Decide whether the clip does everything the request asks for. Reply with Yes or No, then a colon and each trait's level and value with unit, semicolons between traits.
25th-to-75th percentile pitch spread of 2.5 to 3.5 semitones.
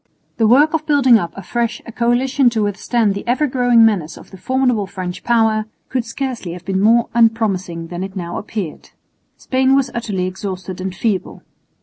No: average, 4.5 semitones